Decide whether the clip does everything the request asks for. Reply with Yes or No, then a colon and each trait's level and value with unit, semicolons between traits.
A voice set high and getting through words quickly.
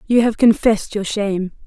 No: high, 210 Hz; average, 180 wpm